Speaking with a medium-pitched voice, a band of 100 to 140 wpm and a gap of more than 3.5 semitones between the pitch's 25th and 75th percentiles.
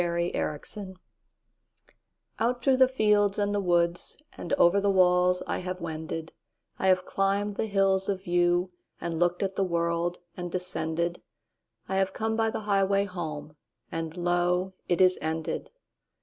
No: medium, 180 Hz; slow, 135 wpm; narrow, 2.5 semitones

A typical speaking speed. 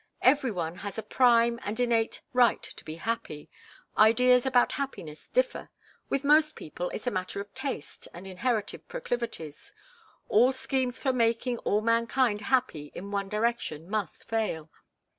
Yes: average, 150 wpm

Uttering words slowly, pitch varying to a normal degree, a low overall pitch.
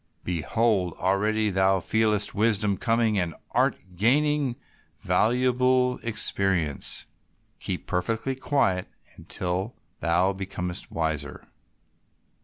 Yes: slow, 85 wpm; average, 4.4 semitones; low, 105 Hz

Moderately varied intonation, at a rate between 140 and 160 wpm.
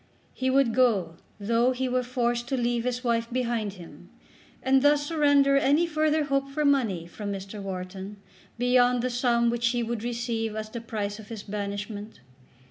No: average, 3.5 semitones; average, 175 wpm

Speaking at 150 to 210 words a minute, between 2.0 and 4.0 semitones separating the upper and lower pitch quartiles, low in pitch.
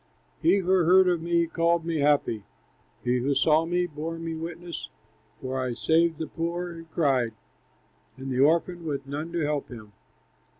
No: average, 170 wpm; average, 3.2 semitones; medium, 165 Hz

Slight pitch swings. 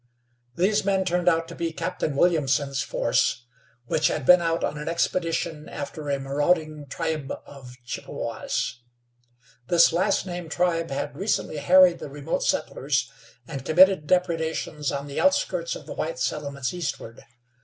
No: average, 3.8 semitones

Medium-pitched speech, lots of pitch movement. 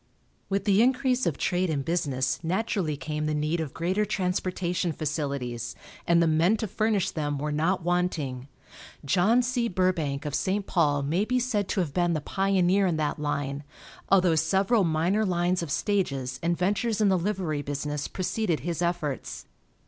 No: medium, 175 Hz; average, 4.6 semitones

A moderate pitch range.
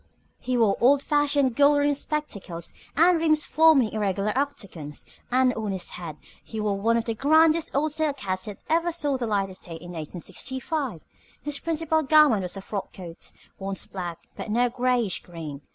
No: wide, 7.1 semitones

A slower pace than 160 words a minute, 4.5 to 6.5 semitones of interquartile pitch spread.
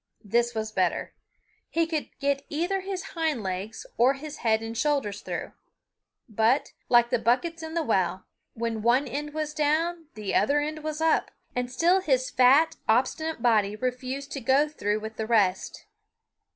No: average, 165 wpm; wide, 5.6 semitones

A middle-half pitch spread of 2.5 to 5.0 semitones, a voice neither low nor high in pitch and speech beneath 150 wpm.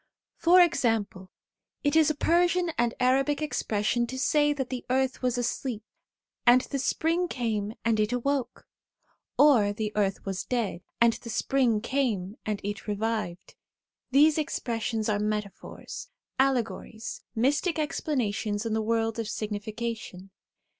No: average, 4.4 semitones; high, 235 Hz; average, 140 wpm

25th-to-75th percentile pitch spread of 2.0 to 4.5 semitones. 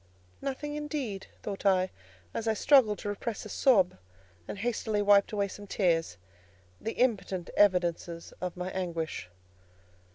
Yes: average, 3.5 semitones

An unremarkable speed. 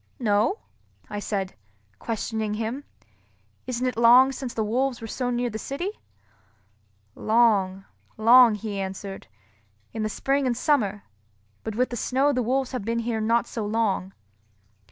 Yes: average, 150 wpm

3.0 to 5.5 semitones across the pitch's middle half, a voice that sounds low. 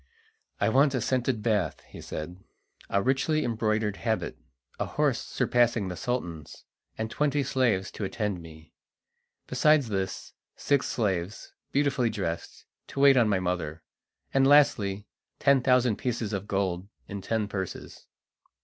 Yes: average, 5.1 semitones; low, 110 Hz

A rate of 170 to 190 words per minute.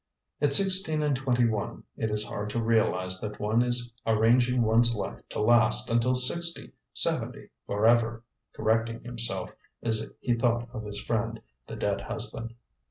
No: average, 155 wpm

